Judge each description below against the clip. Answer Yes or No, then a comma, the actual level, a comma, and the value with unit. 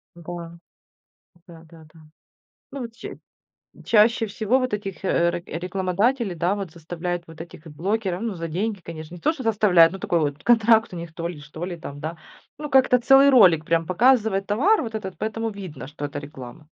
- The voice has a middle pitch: Yes, medium, 180 Hz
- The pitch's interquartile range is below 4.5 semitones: No, average, 5.2 semitones